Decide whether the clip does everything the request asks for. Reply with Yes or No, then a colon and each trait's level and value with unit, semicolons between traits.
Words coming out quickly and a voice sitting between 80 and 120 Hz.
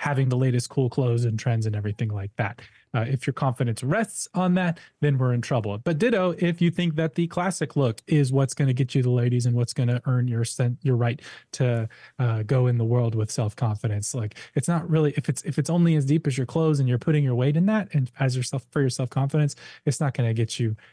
No: fast, 260 wpm; low, 135 Hz